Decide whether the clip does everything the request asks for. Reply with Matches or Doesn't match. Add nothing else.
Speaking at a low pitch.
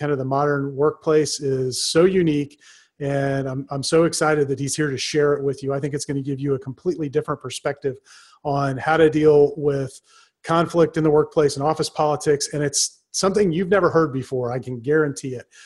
Doesn't match